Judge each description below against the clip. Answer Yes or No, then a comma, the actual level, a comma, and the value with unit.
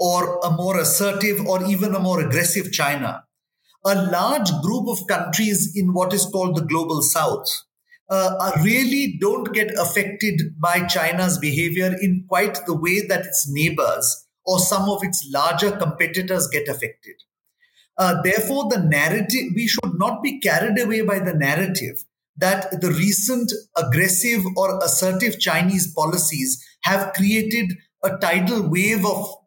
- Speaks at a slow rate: No, average, 145 wpm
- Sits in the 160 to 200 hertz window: Yes, high, 190 Hz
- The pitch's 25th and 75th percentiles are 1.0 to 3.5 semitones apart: Yes, average, 2.9 semitones